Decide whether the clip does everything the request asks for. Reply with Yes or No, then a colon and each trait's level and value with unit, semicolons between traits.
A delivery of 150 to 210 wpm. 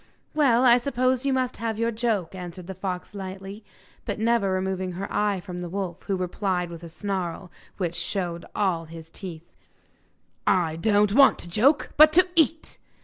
Yes: average, 175 wpm